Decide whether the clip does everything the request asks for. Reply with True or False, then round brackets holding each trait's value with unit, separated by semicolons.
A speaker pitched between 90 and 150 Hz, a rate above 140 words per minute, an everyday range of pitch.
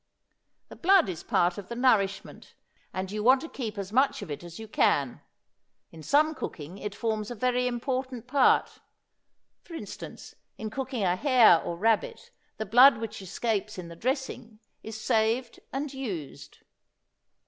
False (225 Hz; 165 wpm; 4.6 semitones)